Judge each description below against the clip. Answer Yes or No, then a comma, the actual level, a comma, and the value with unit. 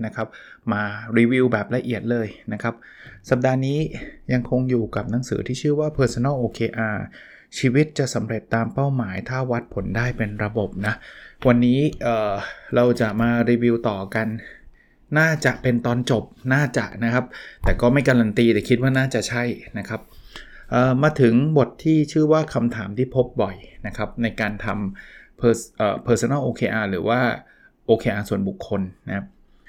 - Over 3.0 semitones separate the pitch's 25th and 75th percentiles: No, average, 2.7 semitones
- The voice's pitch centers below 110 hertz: No, low, 120 Hz